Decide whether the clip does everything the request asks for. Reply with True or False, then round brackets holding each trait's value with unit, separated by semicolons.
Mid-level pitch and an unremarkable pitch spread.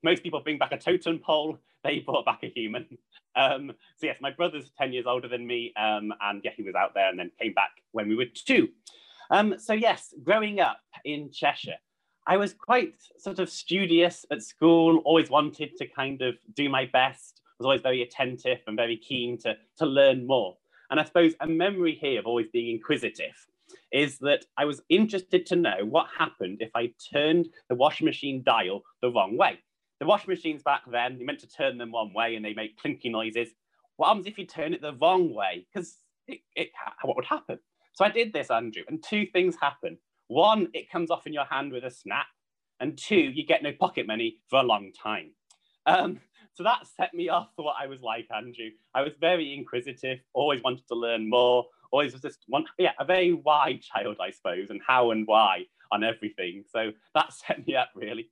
False (150 Hz; 6.8 semitones)